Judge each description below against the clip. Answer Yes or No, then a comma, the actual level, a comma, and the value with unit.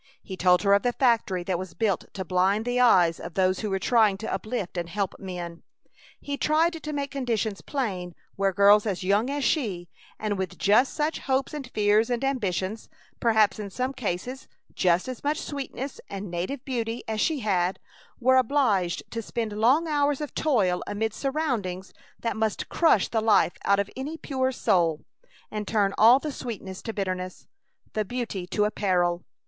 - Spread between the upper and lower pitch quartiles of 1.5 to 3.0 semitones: No, average, 5.3 semitones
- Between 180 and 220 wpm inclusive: Yes, average, 185 wpm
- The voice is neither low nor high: No, high, 215 Hz